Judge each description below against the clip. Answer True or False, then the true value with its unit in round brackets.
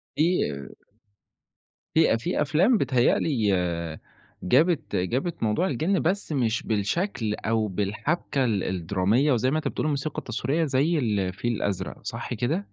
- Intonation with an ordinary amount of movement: False (6.8 semitones)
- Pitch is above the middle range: False (125 Hz)